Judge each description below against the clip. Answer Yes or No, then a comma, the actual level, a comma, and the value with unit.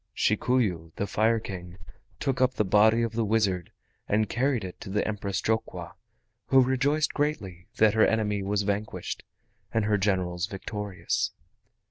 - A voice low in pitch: Yes, low, 105 Hz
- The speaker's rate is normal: Yes, average, 150 wpm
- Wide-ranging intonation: No, average, 2.9 semitones